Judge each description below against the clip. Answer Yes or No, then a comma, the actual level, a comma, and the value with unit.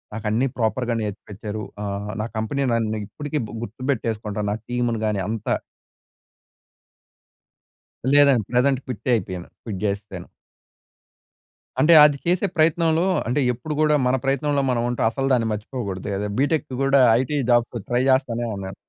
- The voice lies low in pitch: Yes, low, 120 Hz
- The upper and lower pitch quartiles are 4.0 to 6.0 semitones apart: Yes, average, 4.6 semitones